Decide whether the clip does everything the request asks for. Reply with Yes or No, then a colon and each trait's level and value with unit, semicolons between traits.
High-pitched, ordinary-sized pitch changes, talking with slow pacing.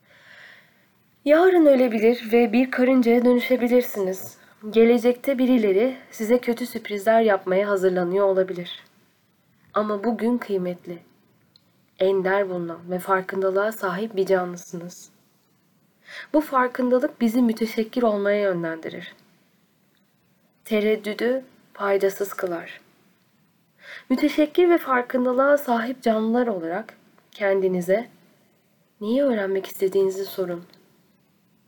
Yes: high, 205 Hz; average, 4.2 semitones; slow, 85 wpm